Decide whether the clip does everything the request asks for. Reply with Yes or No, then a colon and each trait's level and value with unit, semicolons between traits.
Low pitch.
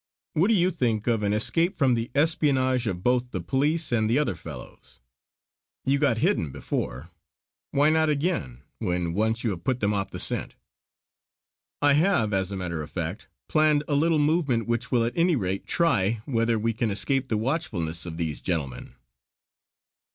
Yes: low, 120 Hz